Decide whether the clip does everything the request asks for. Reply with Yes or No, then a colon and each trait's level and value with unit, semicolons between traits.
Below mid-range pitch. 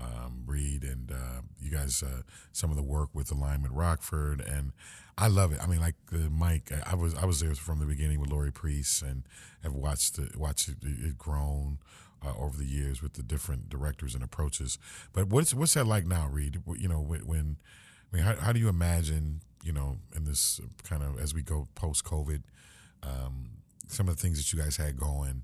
Yes: very low, 75 Hz